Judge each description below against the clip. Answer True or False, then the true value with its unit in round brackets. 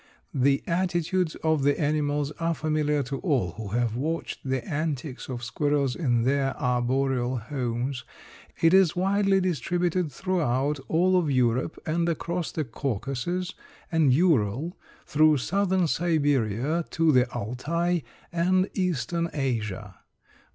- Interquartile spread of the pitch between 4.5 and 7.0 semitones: True (4.9 semitones)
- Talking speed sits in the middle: False (125 wpm)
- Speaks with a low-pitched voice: False (150 Hz)